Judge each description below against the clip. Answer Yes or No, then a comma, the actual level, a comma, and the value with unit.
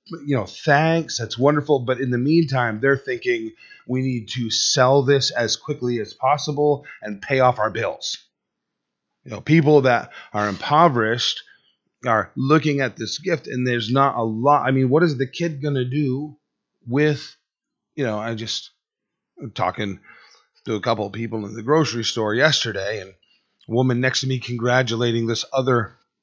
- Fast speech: No, average, 175 wpm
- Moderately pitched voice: No, low, 130 Hz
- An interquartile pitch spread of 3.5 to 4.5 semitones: Yes, average, 4.1 semitones